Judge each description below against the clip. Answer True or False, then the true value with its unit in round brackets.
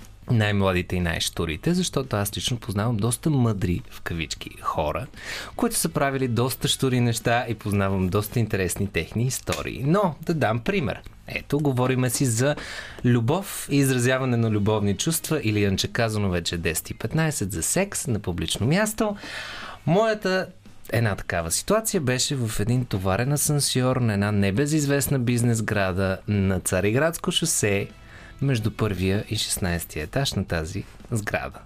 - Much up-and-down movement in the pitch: True (5.8 semitones)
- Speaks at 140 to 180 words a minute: True (145 wpm)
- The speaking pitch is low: True (115 Hz)